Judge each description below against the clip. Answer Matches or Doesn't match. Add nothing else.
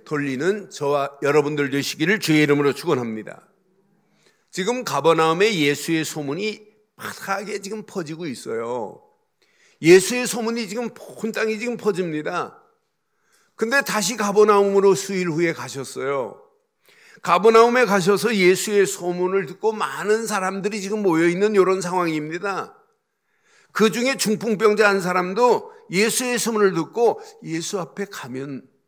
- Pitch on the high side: Matches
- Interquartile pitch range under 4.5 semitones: Doesn't match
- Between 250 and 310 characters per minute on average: Matches